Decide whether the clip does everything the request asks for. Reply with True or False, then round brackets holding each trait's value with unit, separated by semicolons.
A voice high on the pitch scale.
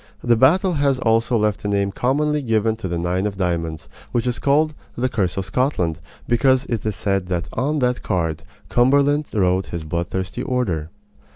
False (110 Hz)